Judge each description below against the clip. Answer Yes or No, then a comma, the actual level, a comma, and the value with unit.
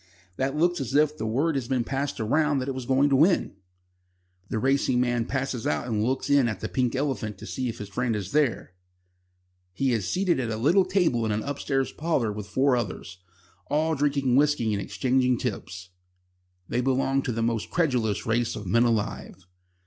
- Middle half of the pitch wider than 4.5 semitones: No, average, 4.0 semitones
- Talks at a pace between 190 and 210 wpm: Yes, average, 195 wpm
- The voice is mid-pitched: No, low, 130 Hz